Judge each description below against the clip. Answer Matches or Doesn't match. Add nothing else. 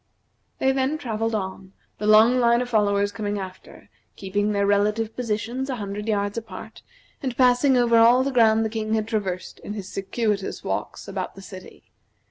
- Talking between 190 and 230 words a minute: Doesn't match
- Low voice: Doesn't match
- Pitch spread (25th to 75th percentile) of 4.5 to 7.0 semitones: Doesn't match